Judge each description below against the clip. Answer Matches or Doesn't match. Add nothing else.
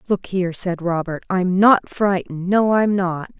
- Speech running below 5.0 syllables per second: Matches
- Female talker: Matches